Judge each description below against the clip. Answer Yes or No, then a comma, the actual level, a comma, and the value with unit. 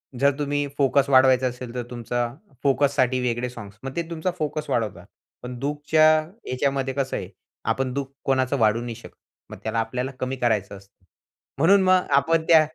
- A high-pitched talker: No, low, 130 Hz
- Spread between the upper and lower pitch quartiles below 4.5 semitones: Yes, average, 2.9 semitones